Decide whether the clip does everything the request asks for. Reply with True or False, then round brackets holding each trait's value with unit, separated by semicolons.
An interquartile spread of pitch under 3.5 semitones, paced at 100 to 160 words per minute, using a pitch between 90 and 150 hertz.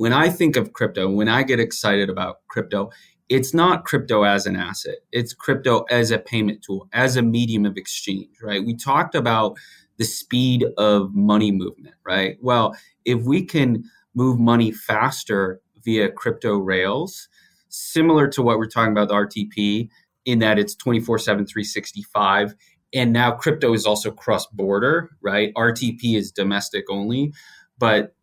True (3.0 semitones; 155 wpm; 110 Hz)